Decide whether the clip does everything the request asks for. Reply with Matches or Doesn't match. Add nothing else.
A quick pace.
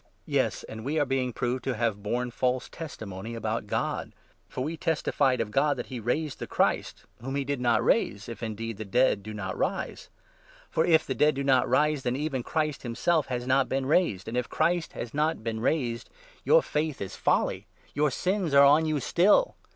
Matches